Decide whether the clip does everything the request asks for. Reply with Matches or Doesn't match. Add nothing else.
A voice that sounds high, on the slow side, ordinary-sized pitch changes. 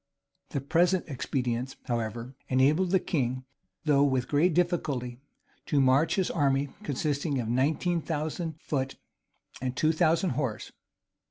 Doesn't match